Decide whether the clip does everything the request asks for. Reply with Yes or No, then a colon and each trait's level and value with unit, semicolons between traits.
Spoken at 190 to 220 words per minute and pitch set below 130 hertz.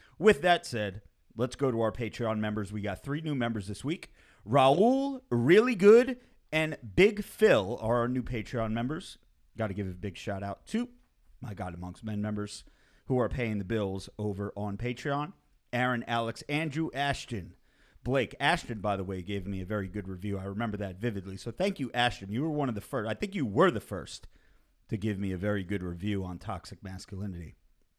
Yes: average, 200 wpm; low, 110 Hz